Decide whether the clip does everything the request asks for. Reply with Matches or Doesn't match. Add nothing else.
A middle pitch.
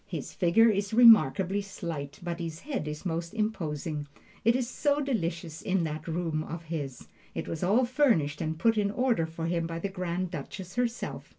Matches